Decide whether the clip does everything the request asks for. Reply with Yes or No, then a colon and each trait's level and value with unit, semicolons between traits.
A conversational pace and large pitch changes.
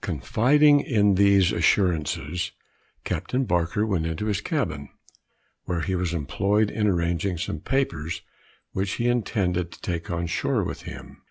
No: average, 145 wpm; average, 3.9 semitones